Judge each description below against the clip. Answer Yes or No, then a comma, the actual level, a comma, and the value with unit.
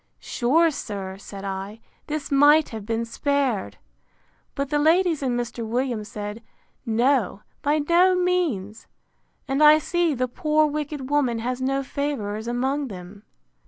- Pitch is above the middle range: Yes, very high, 265 Hz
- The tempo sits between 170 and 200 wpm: No, average, 140 wpm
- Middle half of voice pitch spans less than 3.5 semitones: No, average, 5.2 semitones